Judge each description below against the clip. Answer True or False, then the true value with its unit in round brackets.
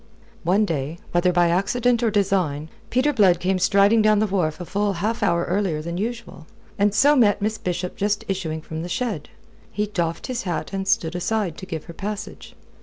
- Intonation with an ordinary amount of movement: True (3.6 semitones)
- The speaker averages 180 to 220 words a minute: True (195 wpm)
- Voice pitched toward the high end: True (195 Hz)